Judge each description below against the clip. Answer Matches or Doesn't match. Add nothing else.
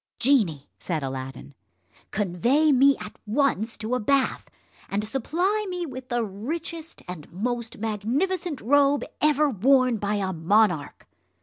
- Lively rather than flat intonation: Matches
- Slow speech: Matches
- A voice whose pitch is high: Matches